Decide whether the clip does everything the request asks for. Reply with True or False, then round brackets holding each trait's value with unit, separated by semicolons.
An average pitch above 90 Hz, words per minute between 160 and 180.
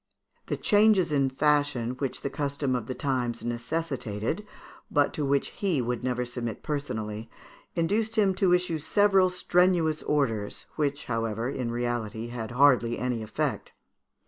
False (135 Hz; 145 wpm)